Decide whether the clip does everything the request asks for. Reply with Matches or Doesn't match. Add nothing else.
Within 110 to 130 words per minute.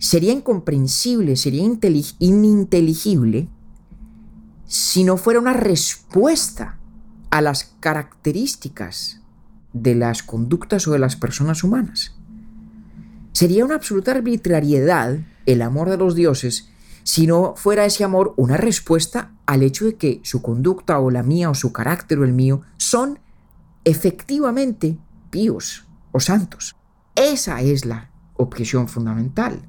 Matches